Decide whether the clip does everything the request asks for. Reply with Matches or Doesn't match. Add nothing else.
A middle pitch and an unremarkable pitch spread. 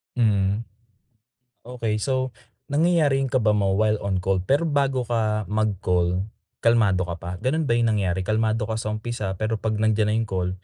Doesn't match